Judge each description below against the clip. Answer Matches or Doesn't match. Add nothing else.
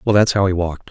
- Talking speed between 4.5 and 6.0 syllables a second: Doesn't match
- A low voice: Matches